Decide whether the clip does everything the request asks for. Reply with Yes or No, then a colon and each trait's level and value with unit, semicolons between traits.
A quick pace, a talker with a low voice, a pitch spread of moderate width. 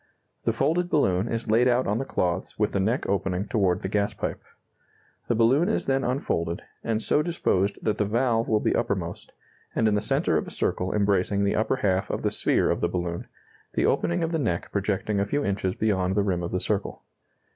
Yes: fast, 215 wpm; low, 105 Hz; average, 4.1 semitones